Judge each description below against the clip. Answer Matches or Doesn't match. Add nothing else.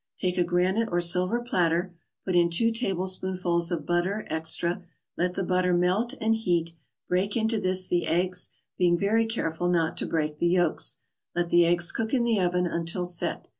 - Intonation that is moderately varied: Doesn't match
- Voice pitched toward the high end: Doesn't match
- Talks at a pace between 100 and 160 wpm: Doesn't match